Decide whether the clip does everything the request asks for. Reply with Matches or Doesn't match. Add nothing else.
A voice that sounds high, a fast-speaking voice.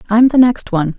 Matches